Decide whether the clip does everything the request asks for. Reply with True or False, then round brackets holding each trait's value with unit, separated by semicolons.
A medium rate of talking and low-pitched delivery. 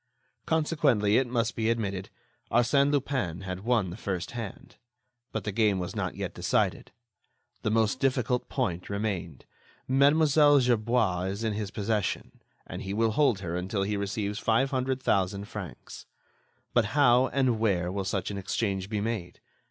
True (160 wpm; 110 Hz)